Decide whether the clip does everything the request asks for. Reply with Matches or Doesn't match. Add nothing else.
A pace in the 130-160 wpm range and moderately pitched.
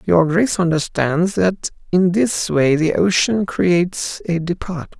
Matches